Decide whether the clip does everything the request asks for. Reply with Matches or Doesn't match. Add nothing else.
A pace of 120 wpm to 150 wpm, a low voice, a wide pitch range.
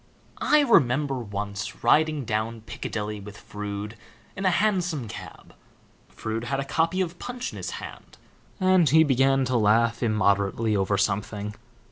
Matches